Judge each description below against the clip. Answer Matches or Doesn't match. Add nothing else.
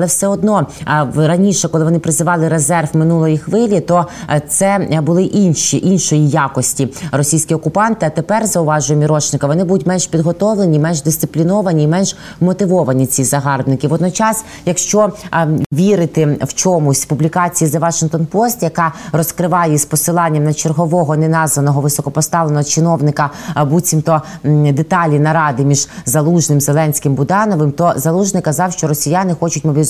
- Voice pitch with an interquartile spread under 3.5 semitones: Matches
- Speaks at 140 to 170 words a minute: Doesn't match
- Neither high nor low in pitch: Matches